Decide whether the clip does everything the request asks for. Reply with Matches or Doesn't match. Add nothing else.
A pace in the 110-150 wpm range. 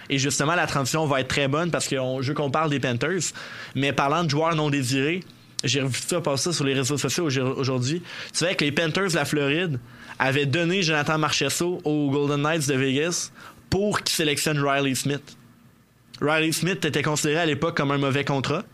Doesn't match